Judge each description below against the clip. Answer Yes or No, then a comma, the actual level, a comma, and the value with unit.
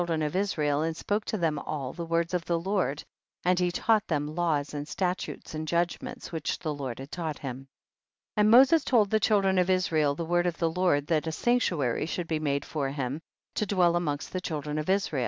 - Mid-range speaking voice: Yes, medium, 165 Hz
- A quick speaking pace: Yes, fast, 225 wpm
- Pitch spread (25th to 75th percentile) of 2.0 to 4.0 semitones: Yes, average, 3.7 semitones